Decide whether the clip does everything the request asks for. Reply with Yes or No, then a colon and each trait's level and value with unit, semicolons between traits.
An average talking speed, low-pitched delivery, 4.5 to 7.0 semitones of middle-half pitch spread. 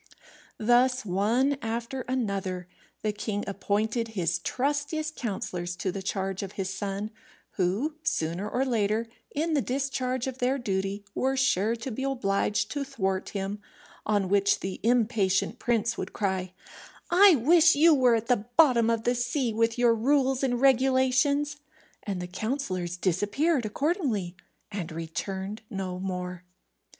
No: average, 145 wpm; high, 225 Hz; average, 5.2 semitones